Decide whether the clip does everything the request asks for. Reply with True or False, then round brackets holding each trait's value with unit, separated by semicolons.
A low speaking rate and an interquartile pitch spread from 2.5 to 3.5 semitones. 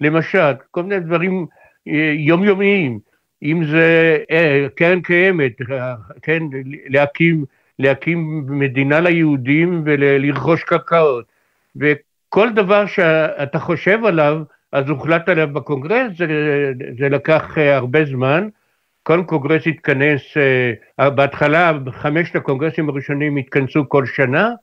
True (95 wpm; 3.0 semitones)